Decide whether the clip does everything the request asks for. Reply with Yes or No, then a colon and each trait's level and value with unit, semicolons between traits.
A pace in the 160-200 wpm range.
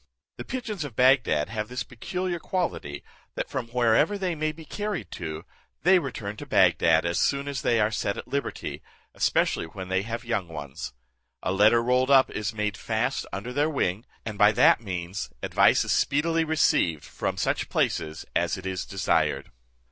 Yes: average, 180 wpm